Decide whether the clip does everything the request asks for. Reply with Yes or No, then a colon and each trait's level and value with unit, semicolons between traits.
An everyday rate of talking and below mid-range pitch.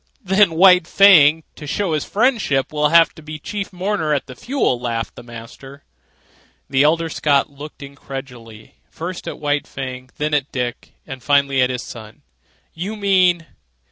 No: average, 165 wpm; medium, 150 Hz